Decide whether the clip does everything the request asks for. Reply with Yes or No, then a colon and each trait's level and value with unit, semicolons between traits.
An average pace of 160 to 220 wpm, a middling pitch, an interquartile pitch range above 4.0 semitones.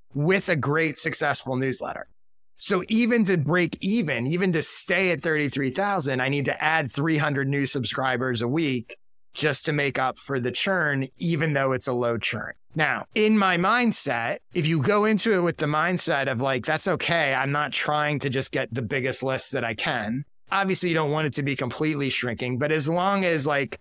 Yes: average, 200 wpm; medium, 150 Hz; average, 4.7 semitones